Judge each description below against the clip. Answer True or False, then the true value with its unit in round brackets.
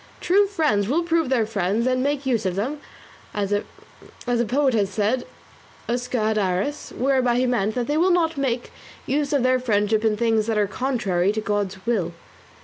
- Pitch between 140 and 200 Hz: False (240 Hz)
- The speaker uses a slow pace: False (185 wpm)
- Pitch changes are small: False (4.5 semitones)